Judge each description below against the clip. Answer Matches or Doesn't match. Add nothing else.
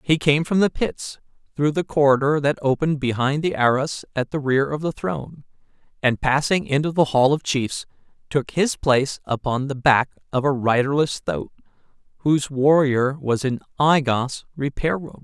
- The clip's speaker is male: Matches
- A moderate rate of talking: Matches